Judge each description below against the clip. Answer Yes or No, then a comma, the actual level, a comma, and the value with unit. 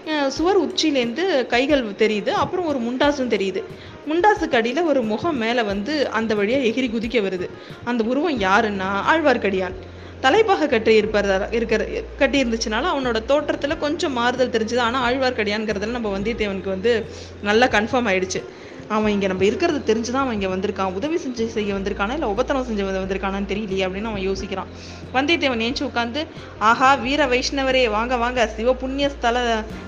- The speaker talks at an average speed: No, fast, 140 wpm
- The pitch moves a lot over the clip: No, average, 4.7 semitones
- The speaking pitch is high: Yes, high, 235 Hz